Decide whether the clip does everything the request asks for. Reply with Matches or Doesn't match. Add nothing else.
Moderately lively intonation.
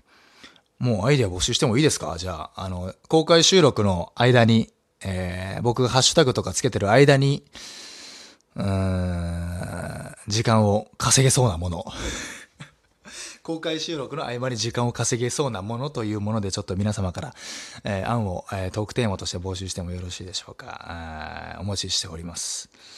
Matches